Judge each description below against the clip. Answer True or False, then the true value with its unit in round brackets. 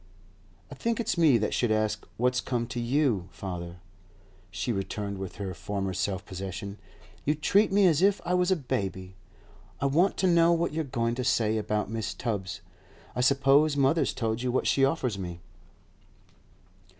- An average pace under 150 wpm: False (175 wpm)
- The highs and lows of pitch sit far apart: True (7.0 semitones)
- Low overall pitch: True (120 Hz)